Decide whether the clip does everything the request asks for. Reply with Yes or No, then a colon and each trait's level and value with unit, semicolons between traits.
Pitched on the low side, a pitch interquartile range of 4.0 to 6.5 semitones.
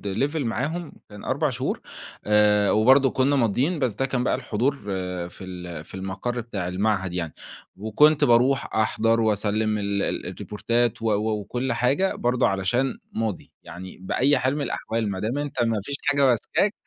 Yes: low, 115 Hz; average, 4.5 semitones